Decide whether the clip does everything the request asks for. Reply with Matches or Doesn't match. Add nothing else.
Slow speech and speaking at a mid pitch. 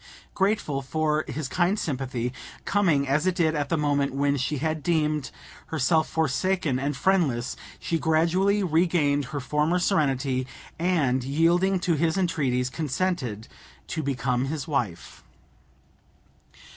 Matches